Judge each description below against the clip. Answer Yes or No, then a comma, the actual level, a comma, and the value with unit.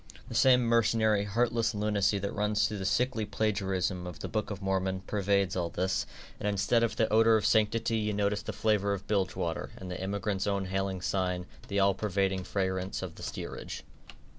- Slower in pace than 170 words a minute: No, average, 190 wpm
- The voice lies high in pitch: No, low, 100 Hz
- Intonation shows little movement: Yes, narrow, 2.1 semitones